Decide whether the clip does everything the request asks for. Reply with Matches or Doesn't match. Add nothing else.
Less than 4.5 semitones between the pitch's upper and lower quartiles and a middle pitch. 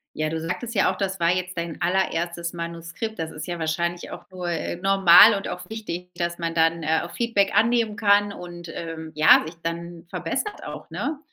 Matches